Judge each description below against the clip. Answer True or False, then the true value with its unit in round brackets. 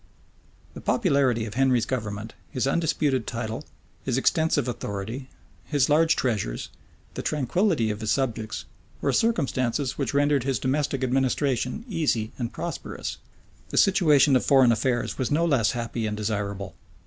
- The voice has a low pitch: True (130 Hz)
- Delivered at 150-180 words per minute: False (140 wpm)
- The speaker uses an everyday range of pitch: True (4.2 semitones)